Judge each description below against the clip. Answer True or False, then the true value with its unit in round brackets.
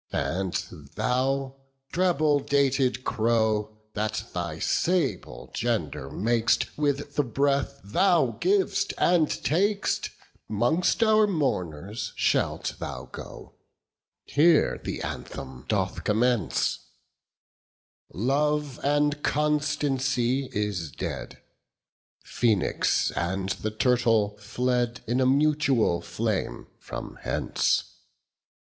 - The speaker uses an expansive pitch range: True (5.8 semitones)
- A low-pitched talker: True (125 Hz)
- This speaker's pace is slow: True (95 wpm)